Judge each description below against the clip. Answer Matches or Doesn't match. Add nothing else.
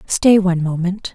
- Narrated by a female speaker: Matches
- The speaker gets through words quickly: Doesn't match